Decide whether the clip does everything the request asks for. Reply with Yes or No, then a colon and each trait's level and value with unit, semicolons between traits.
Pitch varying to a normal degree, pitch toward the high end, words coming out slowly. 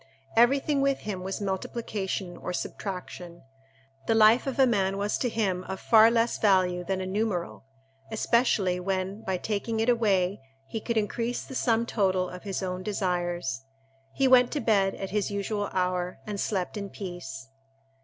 No: average, 3.6 semitones; high, 200 Hz; average, 165 wpm